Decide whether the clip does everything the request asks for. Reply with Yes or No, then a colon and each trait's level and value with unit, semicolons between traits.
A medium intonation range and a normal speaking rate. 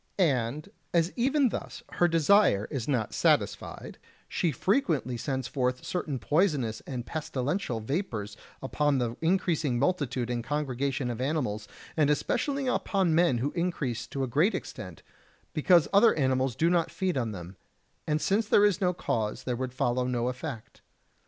No: wide, 6.1 semitones; average, 155 wpm